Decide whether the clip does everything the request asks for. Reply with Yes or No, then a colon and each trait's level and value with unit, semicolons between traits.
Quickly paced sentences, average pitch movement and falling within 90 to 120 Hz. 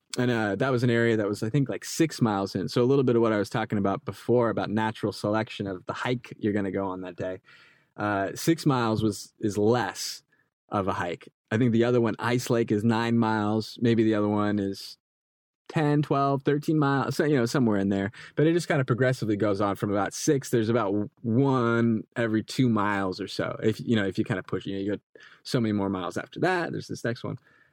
Yes: fast, 245 wpm; average, 3.3 semitones; low, 110 Hz